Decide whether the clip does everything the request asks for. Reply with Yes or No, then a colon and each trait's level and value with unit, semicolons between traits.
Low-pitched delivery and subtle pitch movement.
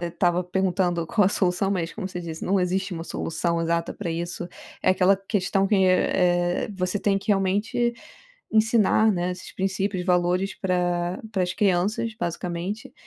No: medium, 185 Hz; narrow, 2.0 semitones